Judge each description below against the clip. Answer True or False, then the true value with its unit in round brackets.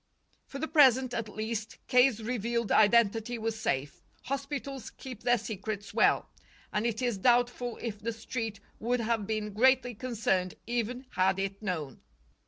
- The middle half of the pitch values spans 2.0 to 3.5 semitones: True (2.8 semitones)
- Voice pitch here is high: True (230 Hz)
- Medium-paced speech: True (150 wpm)